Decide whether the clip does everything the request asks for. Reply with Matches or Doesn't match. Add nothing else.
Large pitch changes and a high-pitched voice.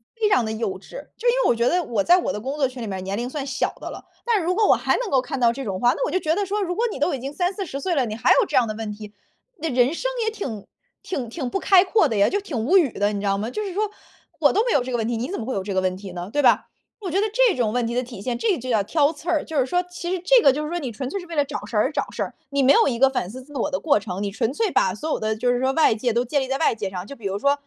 Matches